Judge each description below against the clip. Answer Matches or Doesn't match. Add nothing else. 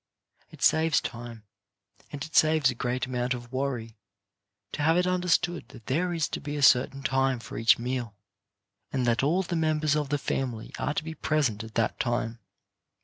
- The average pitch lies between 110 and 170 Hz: Matches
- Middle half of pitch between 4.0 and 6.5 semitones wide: Matches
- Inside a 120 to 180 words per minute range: Doesn't match